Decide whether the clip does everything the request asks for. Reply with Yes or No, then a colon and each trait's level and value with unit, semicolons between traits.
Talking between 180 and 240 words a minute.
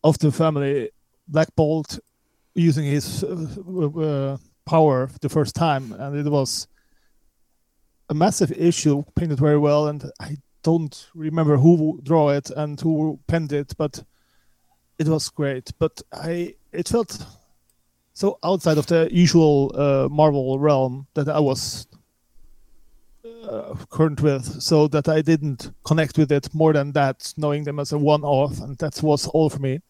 No: average, 155 wpm